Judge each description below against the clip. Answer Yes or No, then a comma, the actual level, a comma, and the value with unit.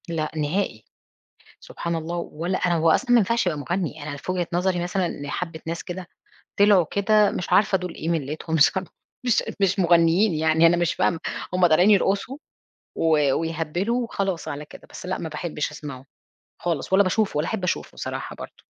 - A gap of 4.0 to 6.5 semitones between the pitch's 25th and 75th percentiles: No, average, 3.1 semitones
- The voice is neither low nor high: Yes, medium, 175 Hz